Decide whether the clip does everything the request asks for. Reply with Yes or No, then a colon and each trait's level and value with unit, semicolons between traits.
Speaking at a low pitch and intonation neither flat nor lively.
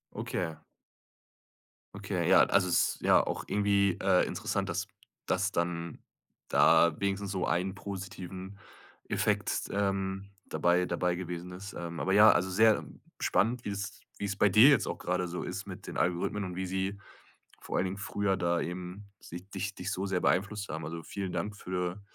No: very low, 95 Hz; narrow, 2.1 semitones